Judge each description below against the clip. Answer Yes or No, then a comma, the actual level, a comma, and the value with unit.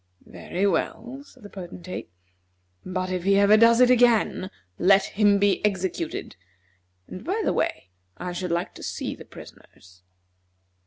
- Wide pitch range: No, average, 3.0 semitones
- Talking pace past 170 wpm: No, average, 150 wpm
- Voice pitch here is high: Yes, high, 195 Hz